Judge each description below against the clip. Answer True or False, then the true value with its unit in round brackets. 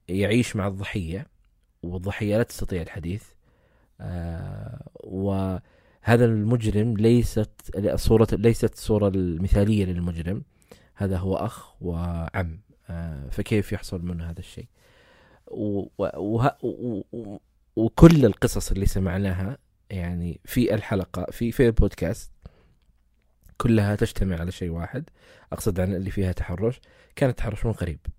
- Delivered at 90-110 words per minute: True (100 wpm)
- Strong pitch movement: False (3.9 semitones)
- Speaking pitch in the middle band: False (100 Hz)